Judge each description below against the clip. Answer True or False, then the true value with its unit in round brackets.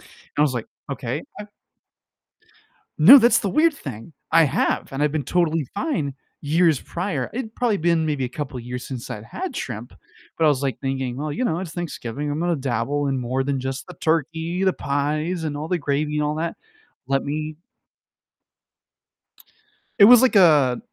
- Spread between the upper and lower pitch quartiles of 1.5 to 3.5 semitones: False (4.3 semitones)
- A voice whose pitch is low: False (150 Hz)